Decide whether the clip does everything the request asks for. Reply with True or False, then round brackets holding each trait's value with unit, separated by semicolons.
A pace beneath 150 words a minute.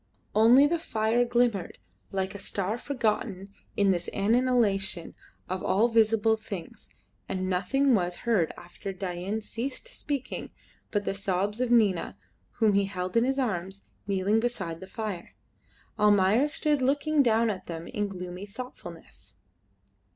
True (140 wpm)